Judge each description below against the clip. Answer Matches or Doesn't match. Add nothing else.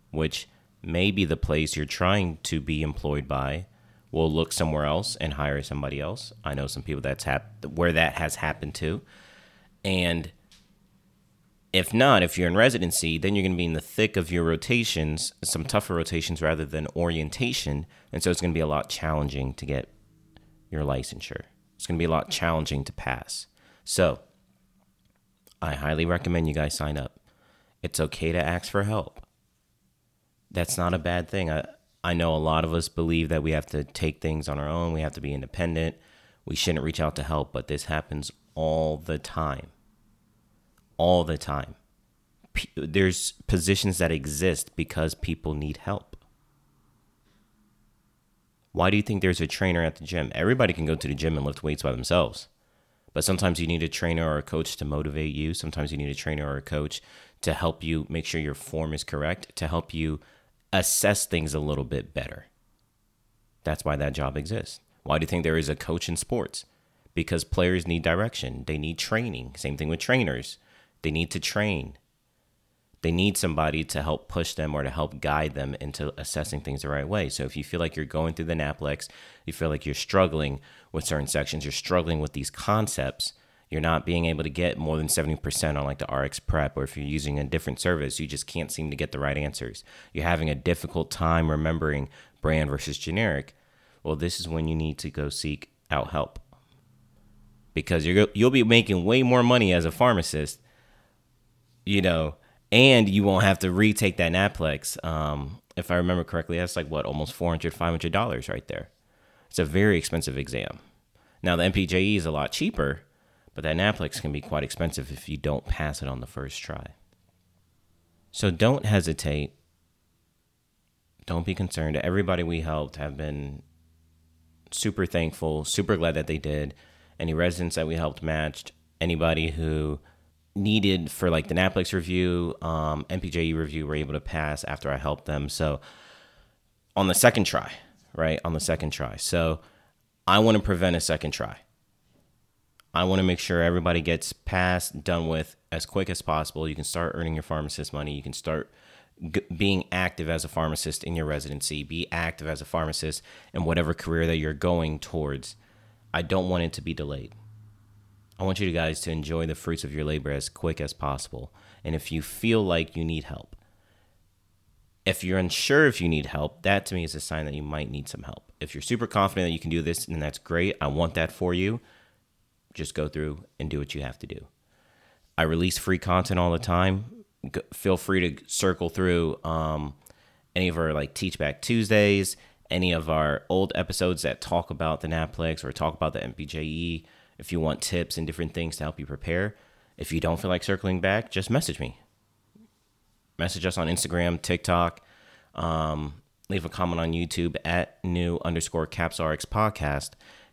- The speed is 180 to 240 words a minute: Matches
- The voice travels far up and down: Doesn't match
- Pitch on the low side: Matches